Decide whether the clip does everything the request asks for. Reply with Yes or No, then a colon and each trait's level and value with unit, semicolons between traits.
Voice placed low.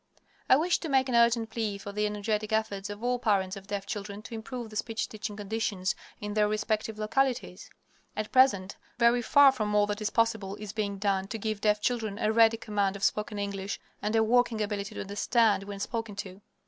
No: high, 215 Hz